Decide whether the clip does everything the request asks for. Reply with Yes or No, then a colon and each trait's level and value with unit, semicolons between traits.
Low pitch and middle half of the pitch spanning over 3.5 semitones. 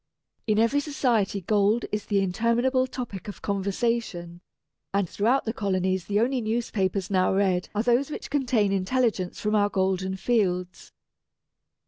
No: high, 205 Hz; average, 3.9 semitones